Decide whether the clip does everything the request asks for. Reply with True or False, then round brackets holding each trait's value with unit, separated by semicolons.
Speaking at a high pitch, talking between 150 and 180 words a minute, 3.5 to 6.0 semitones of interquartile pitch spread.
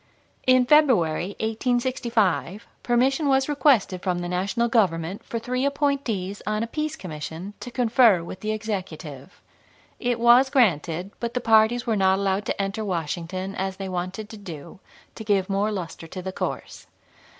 True (205 Hz; 160 wpm; 4.7 semitones)